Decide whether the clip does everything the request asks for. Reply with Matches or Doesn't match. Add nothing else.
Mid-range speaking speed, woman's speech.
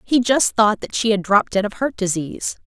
Doesn't match